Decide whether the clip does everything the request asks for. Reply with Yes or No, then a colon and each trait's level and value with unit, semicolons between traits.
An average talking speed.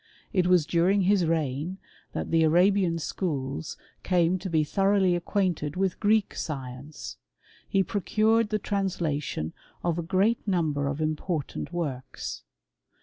No: slow, 130 wpm